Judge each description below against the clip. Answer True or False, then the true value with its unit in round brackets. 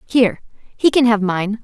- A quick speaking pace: False (145 wpm)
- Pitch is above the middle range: True (215 Hz)